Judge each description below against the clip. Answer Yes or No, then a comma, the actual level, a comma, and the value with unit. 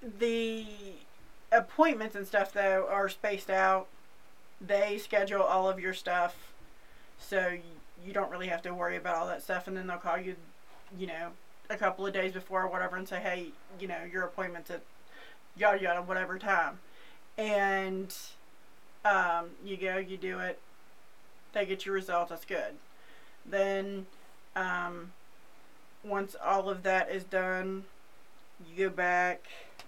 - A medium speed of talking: Yes, average, 150 wpm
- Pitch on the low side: No, high, 190 Hz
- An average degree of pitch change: No, narrow, 1.7 semitones